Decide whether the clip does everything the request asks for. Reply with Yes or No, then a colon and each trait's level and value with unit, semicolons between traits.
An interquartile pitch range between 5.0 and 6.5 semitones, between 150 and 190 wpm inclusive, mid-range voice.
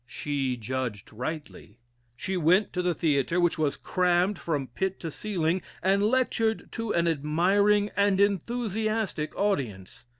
No: wide, 5.5 semitones; slow, 135 wpm; medium, 180 Hz